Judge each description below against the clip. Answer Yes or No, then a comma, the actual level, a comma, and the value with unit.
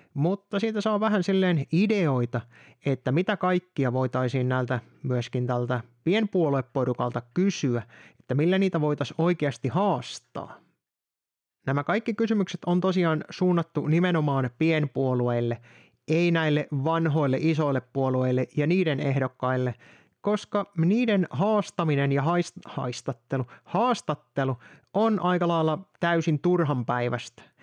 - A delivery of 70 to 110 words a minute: Yes, average, 105 wpm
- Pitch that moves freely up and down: Yes, wide, 5.9 semitones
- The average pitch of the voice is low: No, medium, 150 Hz